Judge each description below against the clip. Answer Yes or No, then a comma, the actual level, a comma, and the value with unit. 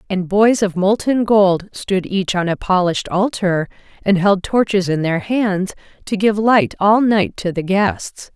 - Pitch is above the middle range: Yes, high, 195 Hz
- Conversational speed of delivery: Yes, average, 180 wpm